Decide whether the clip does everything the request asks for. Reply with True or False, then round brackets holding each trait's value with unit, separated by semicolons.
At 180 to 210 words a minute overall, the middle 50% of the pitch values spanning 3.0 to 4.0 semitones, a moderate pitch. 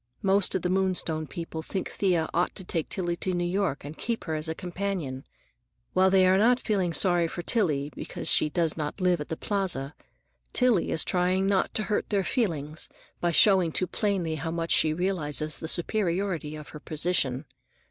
True (190 wpm; 3.3 semitones; 175 Hz)